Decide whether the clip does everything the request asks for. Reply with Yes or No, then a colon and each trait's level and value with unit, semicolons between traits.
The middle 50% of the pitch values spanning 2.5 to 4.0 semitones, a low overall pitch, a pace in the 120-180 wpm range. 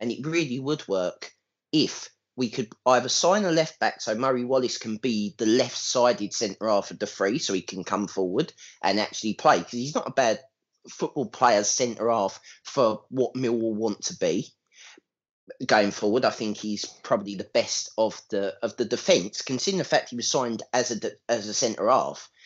No: average, 3.1 semitones; low, 120 Hz; average, 200 wpm